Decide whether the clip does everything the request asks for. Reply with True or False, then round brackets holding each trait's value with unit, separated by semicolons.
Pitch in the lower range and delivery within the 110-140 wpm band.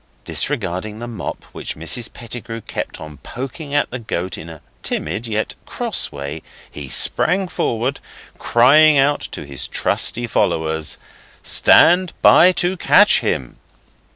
True (115 Hz; 135 wpm)